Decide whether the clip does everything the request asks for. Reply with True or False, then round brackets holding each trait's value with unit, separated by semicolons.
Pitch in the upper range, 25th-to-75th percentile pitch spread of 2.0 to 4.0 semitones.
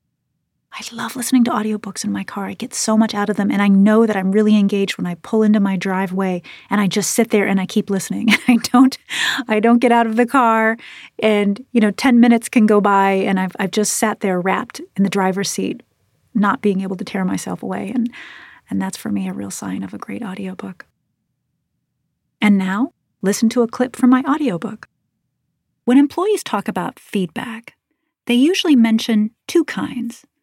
True (215 Hz; 3.7 semitones)